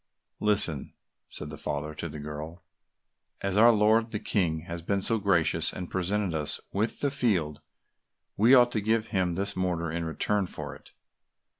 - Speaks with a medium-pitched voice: No, very low, 95 Hz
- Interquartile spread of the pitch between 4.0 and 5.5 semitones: Yes, average, 4.4 semitones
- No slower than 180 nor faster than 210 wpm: No, average, 170 wpm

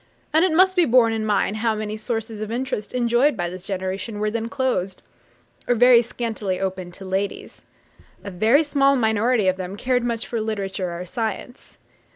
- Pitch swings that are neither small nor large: Yes, average, 4.0 semitones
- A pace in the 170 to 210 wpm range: Yes, average, 185 wpm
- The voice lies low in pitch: No, high, 220 Hz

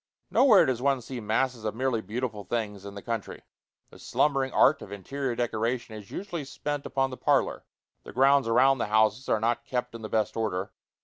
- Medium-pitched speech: No, low, 120 Hz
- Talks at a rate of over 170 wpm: Yes, average, 195 wpm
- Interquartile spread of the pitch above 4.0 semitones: No, average, 3.5 semitones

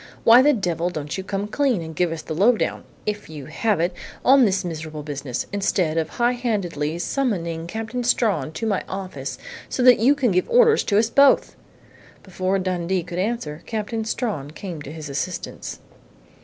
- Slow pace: No, average, 185 wpm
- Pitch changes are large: Yes, wide, 5.9 semitones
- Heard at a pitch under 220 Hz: Yes, high, 190 Hz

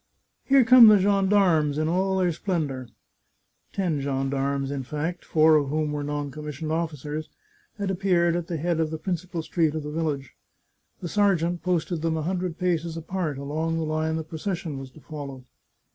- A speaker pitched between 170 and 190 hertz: No, medium, 160 Hz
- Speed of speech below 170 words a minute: No, average, 185 wpm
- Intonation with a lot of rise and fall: No, average, 3.1 semitones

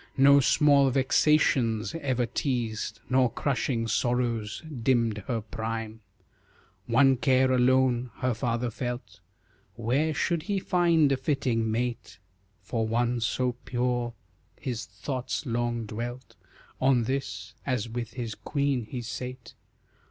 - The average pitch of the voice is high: No, low, 125 Hz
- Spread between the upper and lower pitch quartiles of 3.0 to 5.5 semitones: No, narrow, 2.5 semitones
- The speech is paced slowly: Yes, slow, 120 wpm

